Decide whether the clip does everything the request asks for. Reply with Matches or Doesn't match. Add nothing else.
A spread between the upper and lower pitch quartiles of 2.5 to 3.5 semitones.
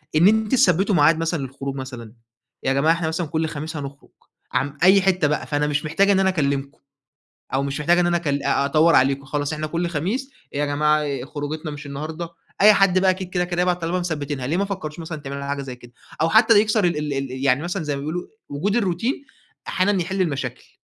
Doesn't match